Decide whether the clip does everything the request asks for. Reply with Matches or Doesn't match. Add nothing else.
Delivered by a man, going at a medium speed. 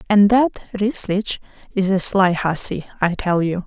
Doesn't match